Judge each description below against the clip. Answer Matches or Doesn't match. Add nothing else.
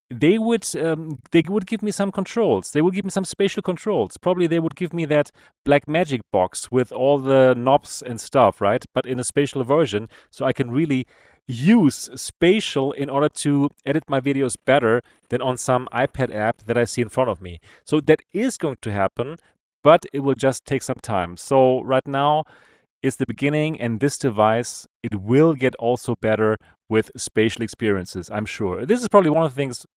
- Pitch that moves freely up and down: Doesn't match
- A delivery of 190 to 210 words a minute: Matches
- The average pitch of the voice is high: Doesn't match